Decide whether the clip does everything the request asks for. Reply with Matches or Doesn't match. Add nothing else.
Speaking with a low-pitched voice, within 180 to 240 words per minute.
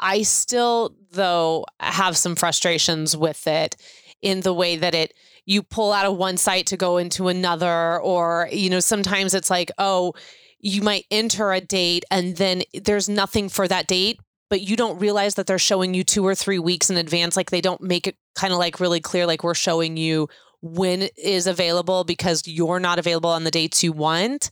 Doesn't match